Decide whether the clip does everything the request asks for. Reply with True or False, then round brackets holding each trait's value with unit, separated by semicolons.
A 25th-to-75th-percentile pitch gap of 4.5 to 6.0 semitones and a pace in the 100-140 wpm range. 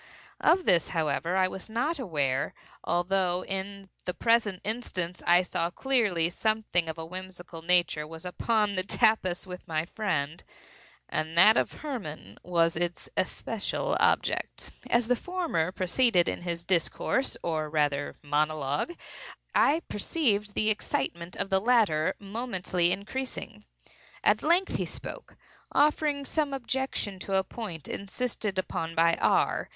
True (5.1 semitones; 135 wpm)